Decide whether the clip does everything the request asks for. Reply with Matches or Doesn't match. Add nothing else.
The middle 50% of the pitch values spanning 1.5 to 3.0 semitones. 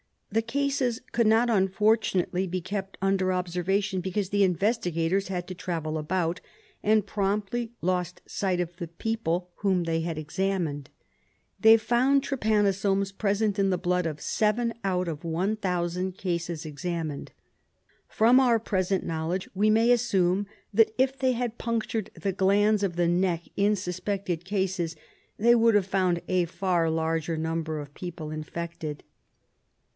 Doesn't match